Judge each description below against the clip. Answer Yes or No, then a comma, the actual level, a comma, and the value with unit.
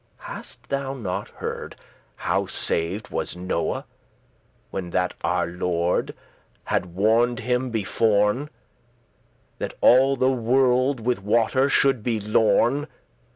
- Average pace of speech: No, slow, 110 wpm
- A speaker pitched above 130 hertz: No, low, 115 Hz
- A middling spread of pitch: Yes, average, 5.0 semitones